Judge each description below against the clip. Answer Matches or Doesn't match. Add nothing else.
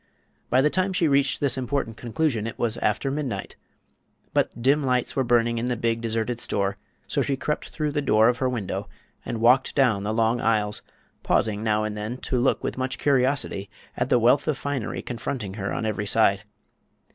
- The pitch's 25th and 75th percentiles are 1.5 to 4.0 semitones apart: Matches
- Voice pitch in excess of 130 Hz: Doesn't match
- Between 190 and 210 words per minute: Matches